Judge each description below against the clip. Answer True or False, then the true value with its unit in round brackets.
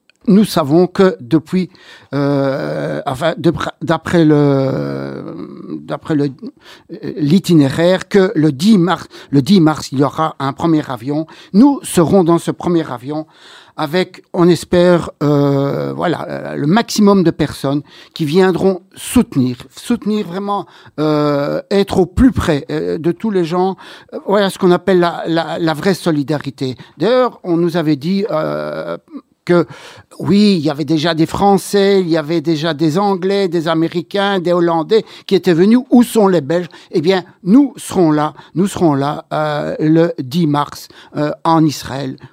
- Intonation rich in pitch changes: False (4.0 semitones)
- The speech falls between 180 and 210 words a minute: False (155 wpm)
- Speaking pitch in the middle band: True (165 Hz)